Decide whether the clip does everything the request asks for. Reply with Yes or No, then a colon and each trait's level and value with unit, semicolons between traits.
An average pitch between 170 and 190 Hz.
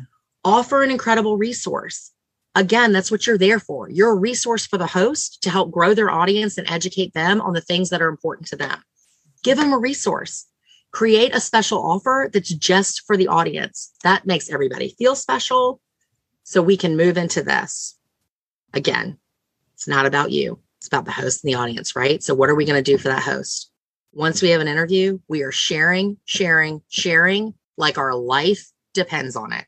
Yes: medium, 185 Hz